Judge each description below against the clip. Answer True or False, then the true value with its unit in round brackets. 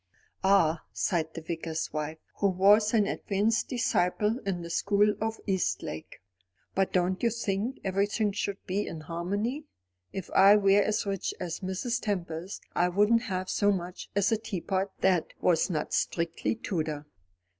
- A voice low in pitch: False (195 Hz)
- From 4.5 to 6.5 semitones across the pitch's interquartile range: False (3.2 semitones)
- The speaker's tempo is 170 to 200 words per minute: False (155 wpm)